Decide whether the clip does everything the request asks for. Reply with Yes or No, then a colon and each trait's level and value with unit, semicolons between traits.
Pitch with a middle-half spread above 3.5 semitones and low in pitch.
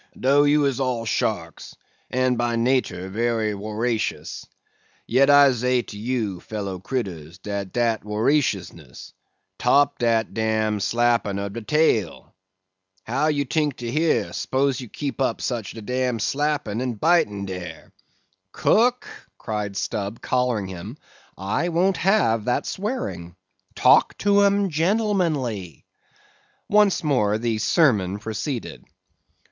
Yes: wide, 5.5 semitones; low, 120 Hz